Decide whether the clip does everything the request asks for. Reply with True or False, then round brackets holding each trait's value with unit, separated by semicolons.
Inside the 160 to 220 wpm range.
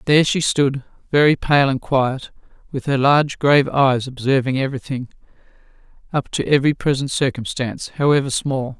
False (135 wpm)